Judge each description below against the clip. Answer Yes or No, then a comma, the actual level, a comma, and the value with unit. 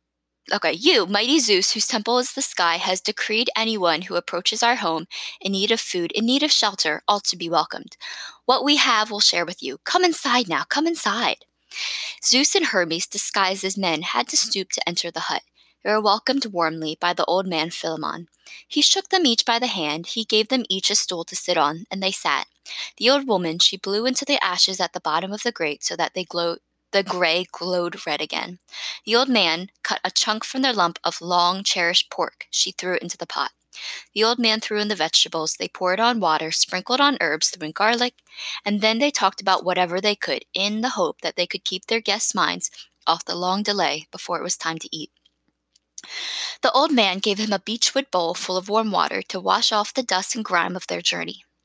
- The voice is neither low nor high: No, high, 195 Hz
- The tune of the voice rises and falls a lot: No, average, 4.8 semitones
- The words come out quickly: Yes, fast, 220 wpm